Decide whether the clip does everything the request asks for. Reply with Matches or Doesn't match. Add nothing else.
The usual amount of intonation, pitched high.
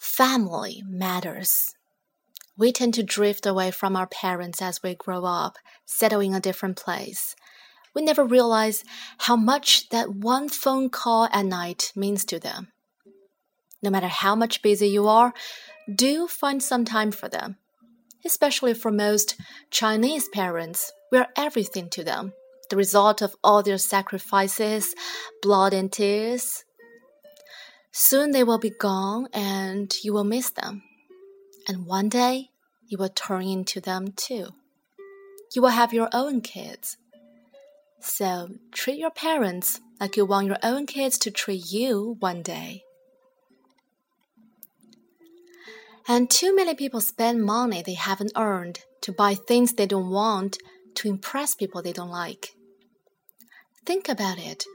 Matches